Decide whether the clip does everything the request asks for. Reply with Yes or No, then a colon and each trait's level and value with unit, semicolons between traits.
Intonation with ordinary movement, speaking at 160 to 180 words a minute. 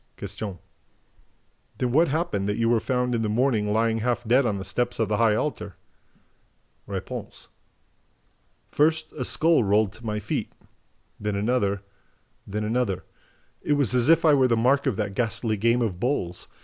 Yes: average, 3.3 semitones; average, 170 wpm